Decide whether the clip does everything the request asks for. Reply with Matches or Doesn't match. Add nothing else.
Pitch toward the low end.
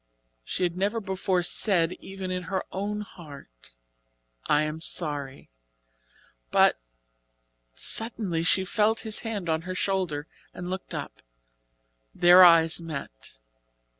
Doesn't match